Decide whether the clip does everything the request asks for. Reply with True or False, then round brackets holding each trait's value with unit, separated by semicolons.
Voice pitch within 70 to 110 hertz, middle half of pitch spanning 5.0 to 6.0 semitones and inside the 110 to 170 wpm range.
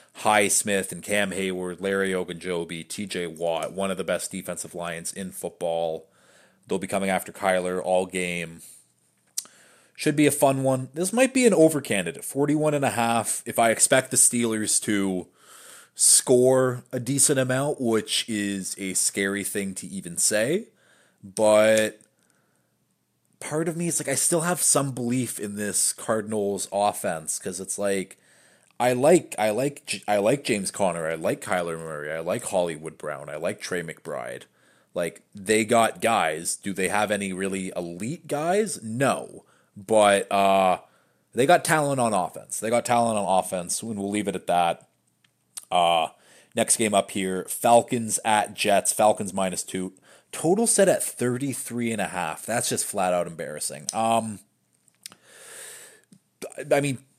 True (105 Hz; 5.5 semitones; 160 wpm)